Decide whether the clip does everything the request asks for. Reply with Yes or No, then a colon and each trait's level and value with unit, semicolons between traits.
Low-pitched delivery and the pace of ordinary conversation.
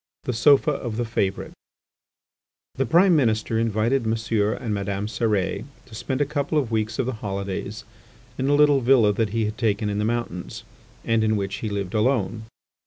Yes: low, 110 Hz; average, 180 wpm